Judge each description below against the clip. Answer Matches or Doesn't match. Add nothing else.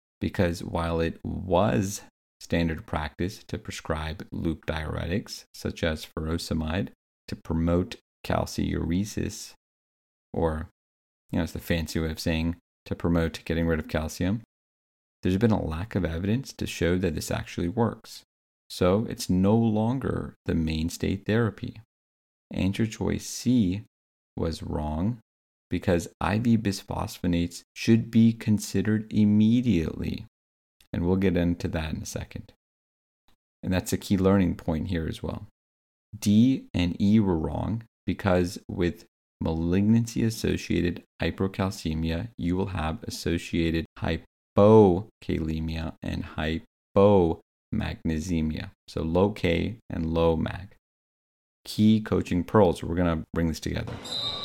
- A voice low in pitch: Matches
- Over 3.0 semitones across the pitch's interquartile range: Matches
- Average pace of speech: Doesn't match